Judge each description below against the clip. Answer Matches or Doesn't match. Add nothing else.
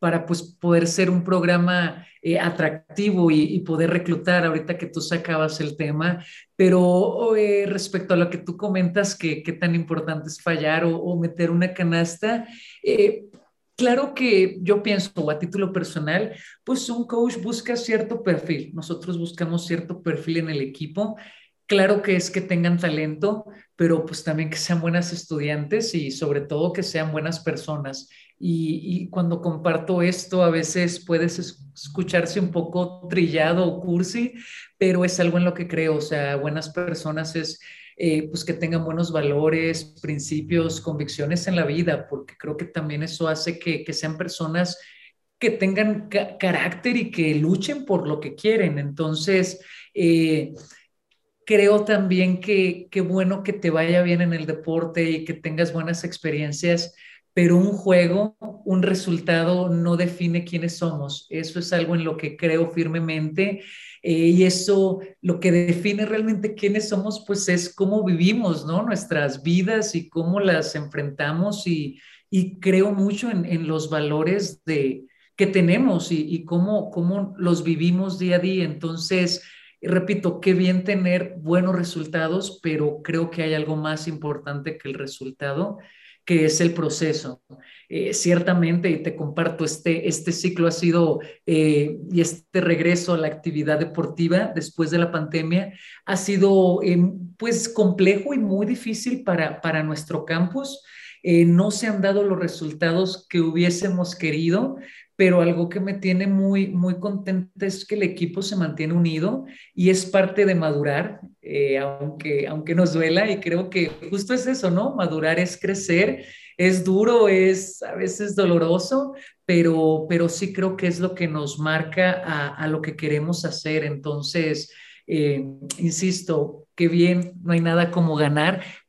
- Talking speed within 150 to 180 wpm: Matches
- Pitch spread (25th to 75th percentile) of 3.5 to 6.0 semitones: Doesn't match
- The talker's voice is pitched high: Doesn't match